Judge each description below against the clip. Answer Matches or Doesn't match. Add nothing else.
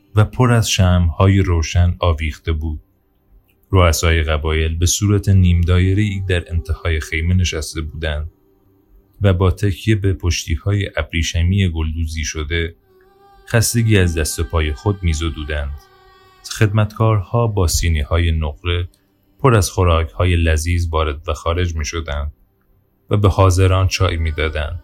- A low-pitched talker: Matches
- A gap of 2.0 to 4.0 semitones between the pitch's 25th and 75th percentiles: Matches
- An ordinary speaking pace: Matches